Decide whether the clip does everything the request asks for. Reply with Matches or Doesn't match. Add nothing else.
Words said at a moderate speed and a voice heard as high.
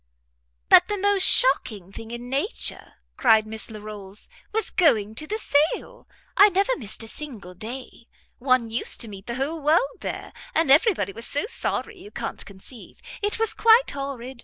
Matches